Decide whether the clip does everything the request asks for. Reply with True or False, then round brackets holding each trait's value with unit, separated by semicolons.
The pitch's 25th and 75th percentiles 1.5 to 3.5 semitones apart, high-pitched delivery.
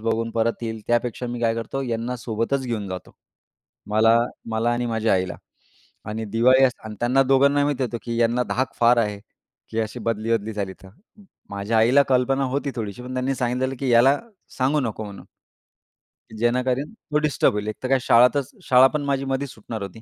False (2.8 semitones; 120 Hz)